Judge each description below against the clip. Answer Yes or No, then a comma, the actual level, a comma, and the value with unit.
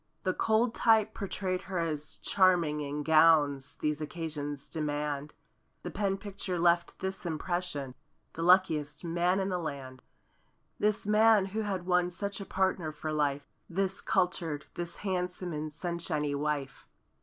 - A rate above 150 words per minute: No, average, 140 wpm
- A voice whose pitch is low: No, medium, 170 Hz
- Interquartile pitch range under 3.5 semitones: No, average, 4.0 semitones